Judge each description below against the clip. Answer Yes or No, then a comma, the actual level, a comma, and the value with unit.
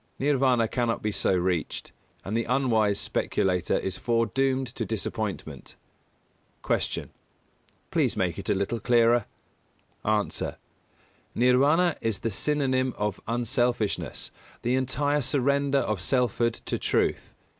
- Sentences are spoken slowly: Yes, slow, 120 wpm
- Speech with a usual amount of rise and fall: Yes, average, 3.7 semitones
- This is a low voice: Yes, low, 120 Hz